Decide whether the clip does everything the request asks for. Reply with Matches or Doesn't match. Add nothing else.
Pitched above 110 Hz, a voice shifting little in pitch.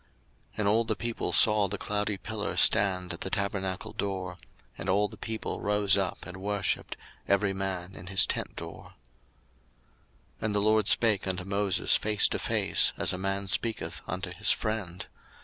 Doesn't match